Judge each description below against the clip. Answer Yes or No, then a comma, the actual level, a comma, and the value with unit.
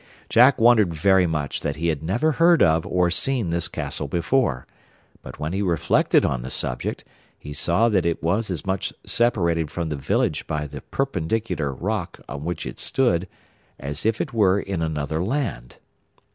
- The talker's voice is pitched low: Yes, very low, 85 Hz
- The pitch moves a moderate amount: No, wide, 6.0 semitones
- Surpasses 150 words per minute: Yes, average, 175 wpm